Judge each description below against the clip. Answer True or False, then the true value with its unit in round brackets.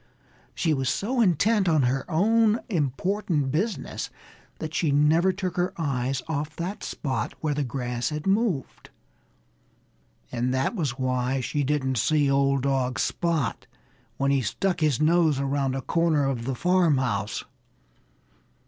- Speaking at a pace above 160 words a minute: False (140 wpm)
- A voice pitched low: False (145 Hz)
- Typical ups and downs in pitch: True (4.6 semitones)